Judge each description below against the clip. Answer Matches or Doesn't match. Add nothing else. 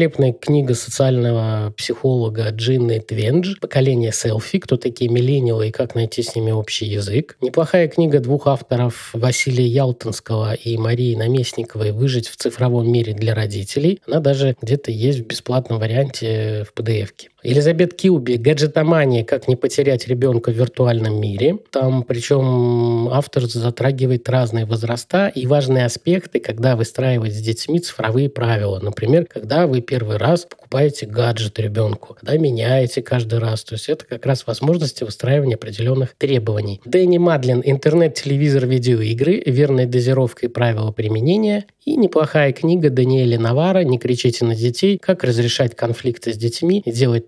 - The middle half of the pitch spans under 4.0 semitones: Matches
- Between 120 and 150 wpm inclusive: Matches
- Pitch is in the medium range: Doesn't match